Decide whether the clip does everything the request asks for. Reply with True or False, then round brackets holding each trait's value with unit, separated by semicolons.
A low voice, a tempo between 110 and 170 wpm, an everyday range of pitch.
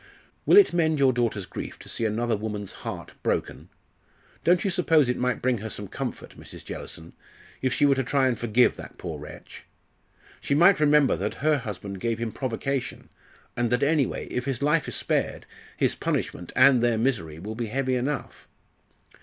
False (125 Hz; 185 wpm; 4.0 semitones)